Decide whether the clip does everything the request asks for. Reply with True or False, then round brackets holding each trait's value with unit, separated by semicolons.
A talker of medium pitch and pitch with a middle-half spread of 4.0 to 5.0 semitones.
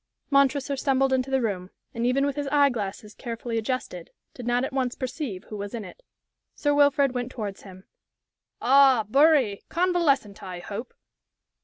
False (255 Hz; 4.6 semitones)